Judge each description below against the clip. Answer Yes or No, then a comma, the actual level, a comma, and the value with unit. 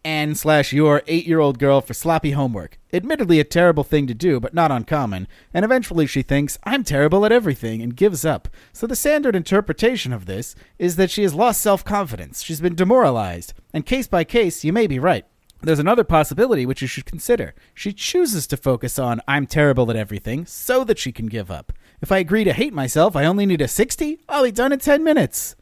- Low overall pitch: No, medium, 155 Hz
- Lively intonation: Yes, wide, 7.3 semitones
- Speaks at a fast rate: Yes, fast, 210 wpm